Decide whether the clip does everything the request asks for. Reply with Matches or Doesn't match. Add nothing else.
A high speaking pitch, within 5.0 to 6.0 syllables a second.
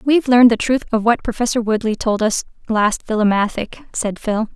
Matches